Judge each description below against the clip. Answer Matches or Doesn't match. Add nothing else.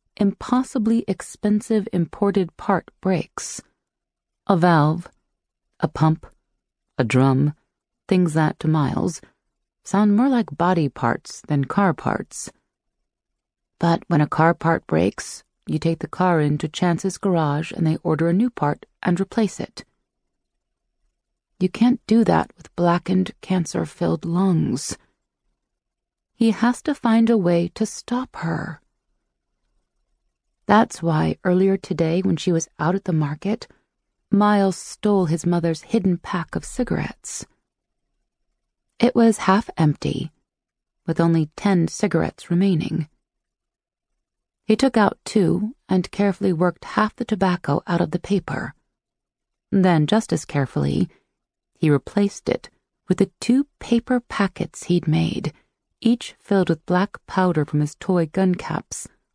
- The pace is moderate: Doesn't match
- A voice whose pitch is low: Doesn't match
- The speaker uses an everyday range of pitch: Matches